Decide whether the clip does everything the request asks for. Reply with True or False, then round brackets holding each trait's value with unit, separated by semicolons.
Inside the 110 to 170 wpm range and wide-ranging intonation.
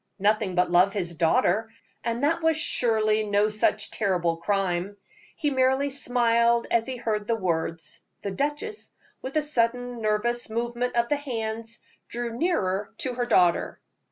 False (155 wpm; 3.6 semitones)